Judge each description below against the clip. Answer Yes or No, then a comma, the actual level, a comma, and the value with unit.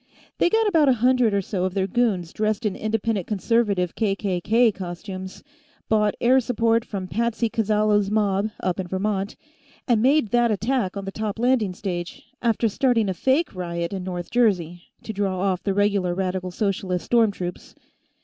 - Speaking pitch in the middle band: No, high, 205 Hz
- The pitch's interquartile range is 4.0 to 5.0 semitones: No, average, 3.5 semitones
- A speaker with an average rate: Yes, average, 170 wpm